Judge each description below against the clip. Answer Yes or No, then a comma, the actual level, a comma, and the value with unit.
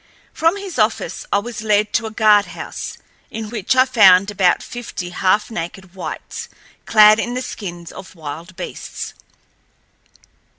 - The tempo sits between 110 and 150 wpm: Yes, average, 140 wpm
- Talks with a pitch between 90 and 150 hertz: No, high, 210 Hz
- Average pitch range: Yes, average, 3.4 semitones